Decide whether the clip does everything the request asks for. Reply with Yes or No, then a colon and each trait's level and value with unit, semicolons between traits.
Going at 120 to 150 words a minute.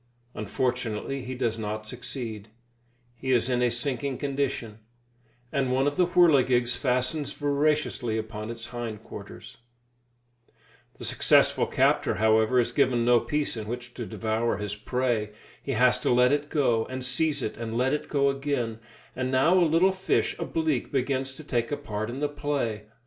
No: average, 170 wpm